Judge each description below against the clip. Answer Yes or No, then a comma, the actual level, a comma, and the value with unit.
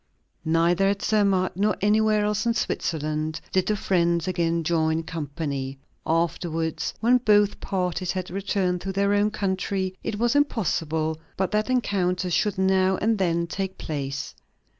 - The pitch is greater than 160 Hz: Yes, medium, 185 Hz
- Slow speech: No, average, 145 wpm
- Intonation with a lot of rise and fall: No, average, 3.7 semitones